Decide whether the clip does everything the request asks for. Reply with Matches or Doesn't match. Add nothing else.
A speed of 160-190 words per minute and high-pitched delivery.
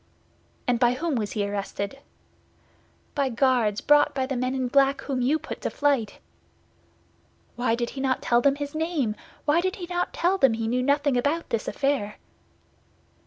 Matches